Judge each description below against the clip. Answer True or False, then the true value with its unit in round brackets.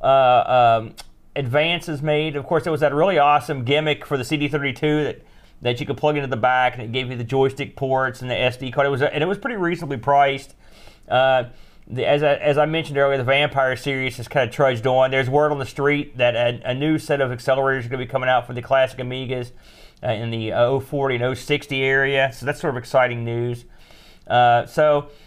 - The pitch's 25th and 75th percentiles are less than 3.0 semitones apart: True (2.6 semitones)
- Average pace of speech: False (230 wpm)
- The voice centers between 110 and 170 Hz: True (135 Hz)